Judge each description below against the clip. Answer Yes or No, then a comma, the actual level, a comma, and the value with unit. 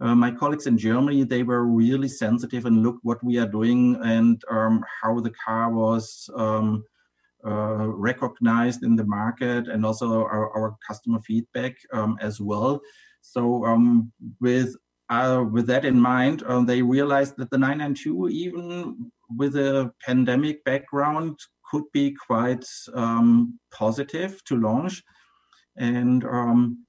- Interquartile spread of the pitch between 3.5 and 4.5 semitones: No, average, 2.8 semitones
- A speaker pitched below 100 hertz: No, low, 120 Hz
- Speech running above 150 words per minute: No, average, 145 wpm